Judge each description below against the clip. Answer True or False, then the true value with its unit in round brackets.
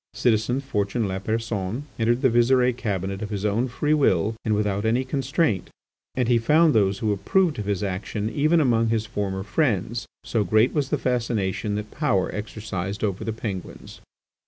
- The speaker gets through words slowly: False (170 wpm)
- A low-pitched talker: True (110 Hz)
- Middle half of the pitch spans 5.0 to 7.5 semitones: False (3.7 semitones)